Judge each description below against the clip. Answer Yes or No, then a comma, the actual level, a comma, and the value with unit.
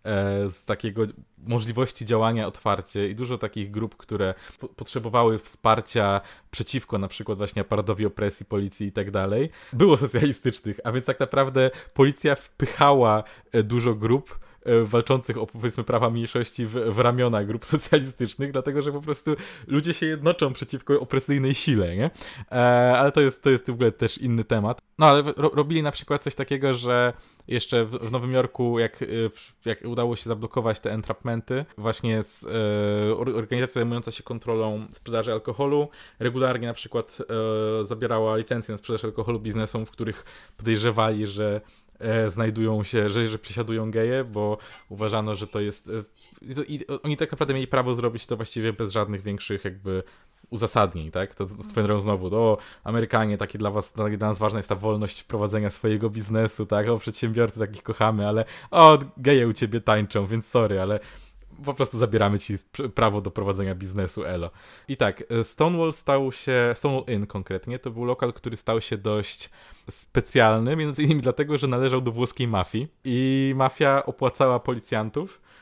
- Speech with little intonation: No, average, 3.3 semitones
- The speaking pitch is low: Yes, low, 115 Hz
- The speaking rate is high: Yes, fast, 165 wpm